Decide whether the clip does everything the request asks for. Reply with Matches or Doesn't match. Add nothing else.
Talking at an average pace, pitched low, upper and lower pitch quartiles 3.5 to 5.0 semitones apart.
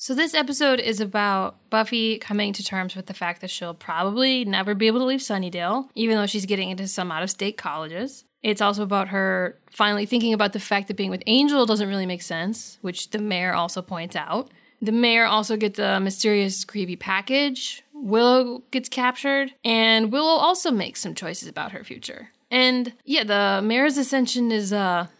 Doesn't match